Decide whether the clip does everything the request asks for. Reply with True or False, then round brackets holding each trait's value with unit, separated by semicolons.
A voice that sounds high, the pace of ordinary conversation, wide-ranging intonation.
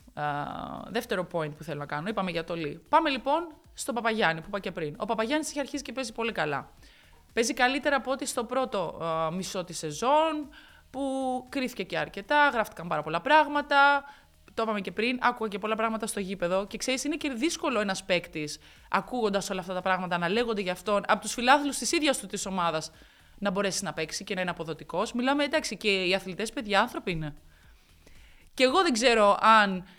False (215 Hz; 205 wpm; 6.9 semitones)